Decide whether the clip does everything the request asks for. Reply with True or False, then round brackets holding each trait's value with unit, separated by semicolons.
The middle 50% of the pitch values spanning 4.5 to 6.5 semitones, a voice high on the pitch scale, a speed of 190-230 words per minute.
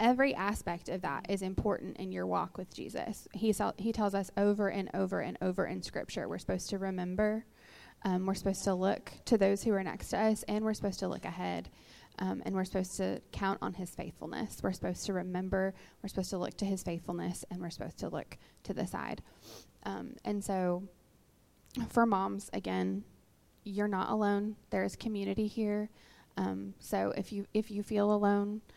False (2.7 semitones; 195 Hz; 195 wpm)